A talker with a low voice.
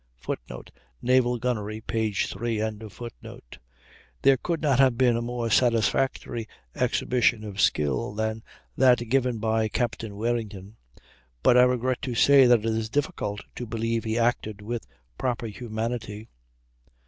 Yes: low, 115 Hz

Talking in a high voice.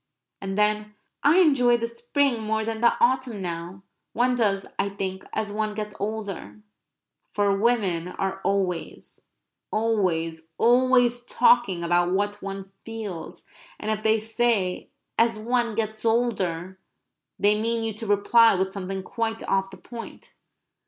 Yes: high, 215 Hz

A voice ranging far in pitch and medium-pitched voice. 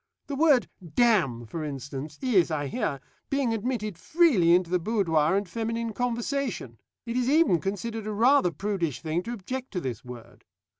No: wide, 6.9 semitones; high, 205 Hz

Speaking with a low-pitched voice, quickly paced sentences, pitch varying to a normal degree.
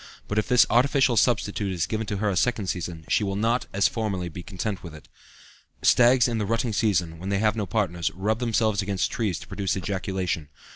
Yes: low, 100 Hz; fast, 210 wpm; average, 3.4 semitones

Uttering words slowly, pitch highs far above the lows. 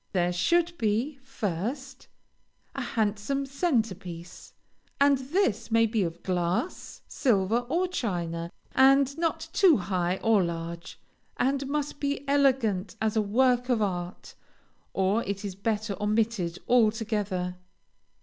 Yes: slow, 125 wpm; wide, 6.3 semitones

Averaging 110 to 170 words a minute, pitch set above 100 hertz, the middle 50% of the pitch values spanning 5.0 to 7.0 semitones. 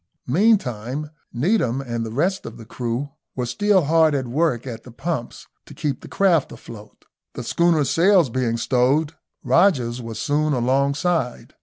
Yes: average, 155 wpm; low, 135 Hz; wide, 5.4 semitones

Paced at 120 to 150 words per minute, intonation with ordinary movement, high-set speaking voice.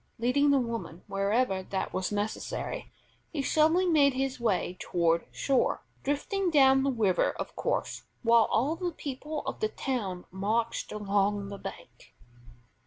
No: average, 145 wpm; wide, 6.0 semitones; high, 235 Hz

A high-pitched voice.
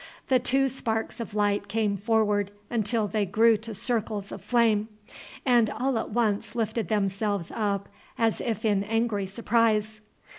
Yes: high, 220 Hz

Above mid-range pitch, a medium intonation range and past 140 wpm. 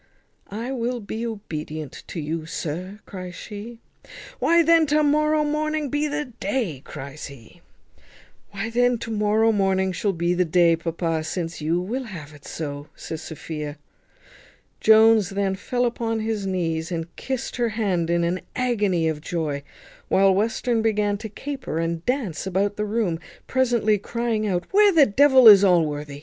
No: high, 200 Hz; wide, 6.0 semitones; average, 160 wpm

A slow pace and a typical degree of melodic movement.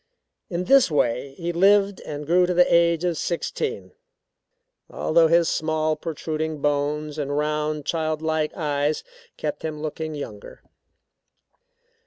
No: slow, 130 wpm; narrow, 2.2 semitones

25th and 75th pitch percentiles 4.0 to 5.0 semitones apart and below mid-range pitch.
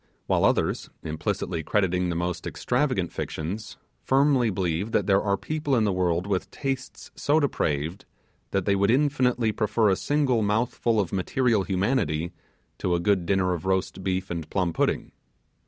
Yes: average, 4.7 semitones; low, 100 Hz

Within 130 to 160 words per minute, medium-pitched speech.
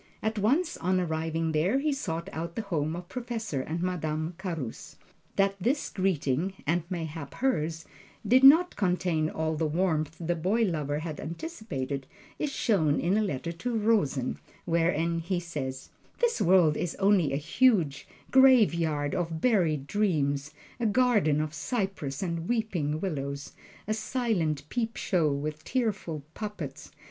Yes: average, 145 wpm; medium, 170 Hz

